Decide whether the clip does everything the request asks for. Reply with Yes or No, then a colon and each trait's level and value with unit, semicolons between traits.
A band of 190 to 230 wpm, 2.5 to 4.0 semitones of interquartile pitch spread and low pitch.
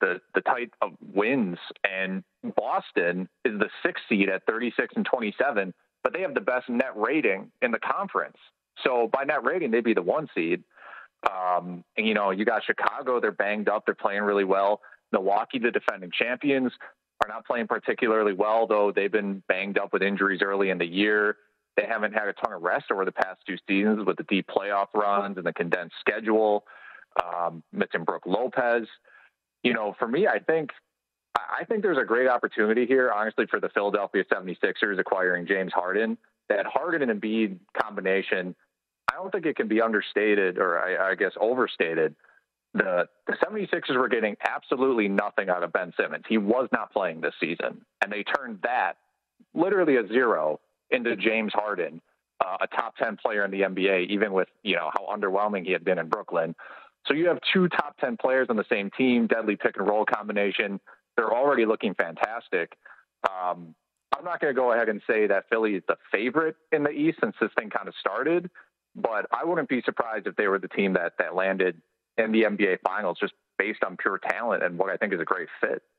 Yes: average, 195 wpm; average, 2.9 semitones; low, 105 Hz